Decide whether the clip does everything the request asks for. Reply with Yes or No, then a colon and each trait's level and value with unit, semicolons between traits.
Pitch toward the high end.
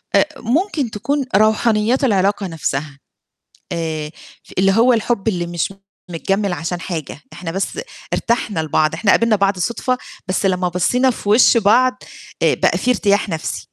Yes: high, 200 Hz